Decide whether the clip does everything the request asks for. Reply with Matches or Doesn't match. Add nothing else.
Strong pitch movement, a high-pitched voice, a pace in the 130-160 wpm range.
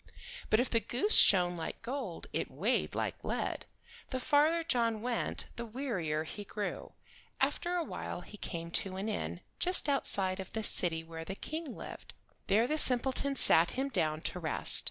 Doesn't match